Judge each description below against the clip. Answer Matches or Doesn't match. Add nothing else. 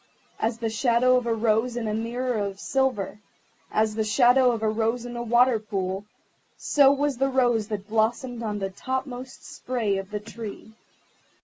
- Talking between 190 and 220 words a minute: Doesn't match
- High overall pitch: Matches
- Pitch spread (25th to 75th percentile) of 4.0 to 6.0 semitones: Doesn't match